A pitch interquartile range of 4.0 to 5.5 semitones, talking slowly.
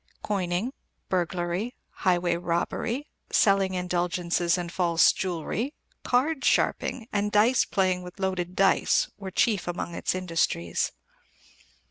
No: average, 2.9 semitones; slow, 110 wpm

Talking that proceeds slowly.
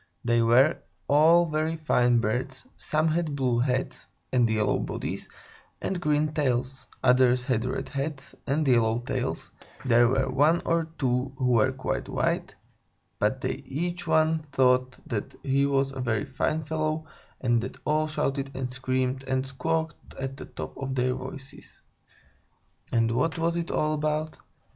No: average, 155 wpm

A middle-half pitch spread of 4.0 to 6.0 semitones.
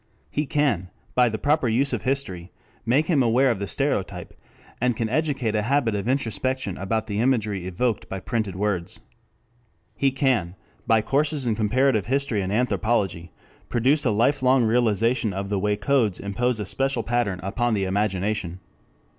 Yes: average, 4.5 semitones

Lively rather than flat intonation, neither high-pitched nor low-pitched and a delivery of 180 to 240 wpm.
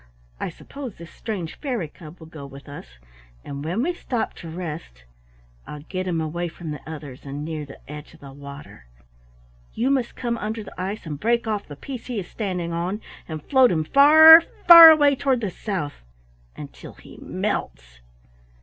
Yes: wide, 7.8 semitones; medium, 175 Hz; average, 185 wpm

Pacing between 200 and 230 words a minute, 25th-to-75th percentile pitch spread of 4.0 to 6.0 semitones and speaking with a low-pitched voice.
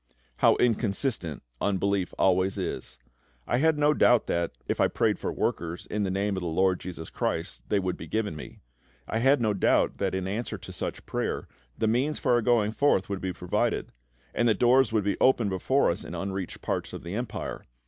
Yes: fast, 205 wpm; average, 4.4 semitones; low, 100 Hz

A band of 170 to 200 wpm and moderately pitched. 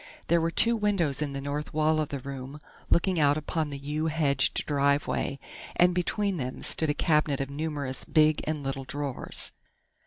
Yes: average, 180 wpm; medium, 150 Hz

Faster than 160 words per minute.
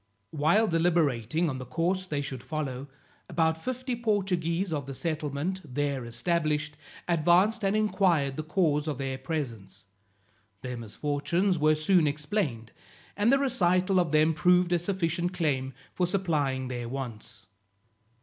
No: average, 140 wpm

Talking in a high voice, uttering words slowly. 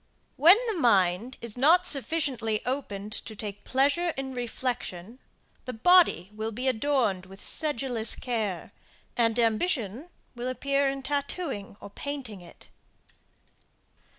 Yes: high, 245 Hz; slow, 125 wpm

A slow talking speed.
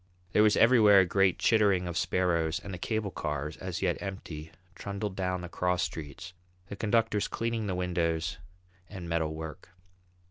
No: average, 165 wpm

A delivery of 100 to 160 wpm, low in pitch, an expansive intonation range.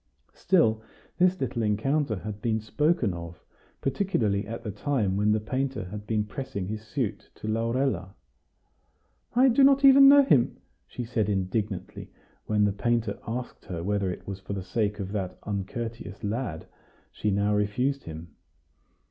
No: average, 155 wpm; low, 110 Hz; average, 4.3 semitones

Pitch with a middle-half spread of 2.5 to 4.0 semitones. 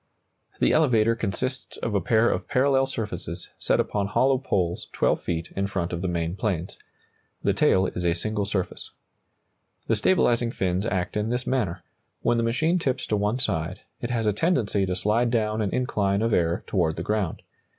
No: average, 4.4 semitones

